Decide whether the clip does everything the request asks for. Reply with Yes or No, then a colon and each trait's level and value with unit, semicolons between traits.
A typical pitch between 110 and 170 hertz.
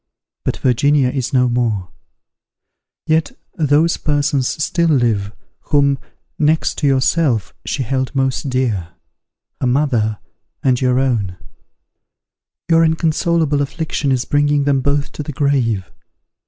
Yes: low, 135 Hz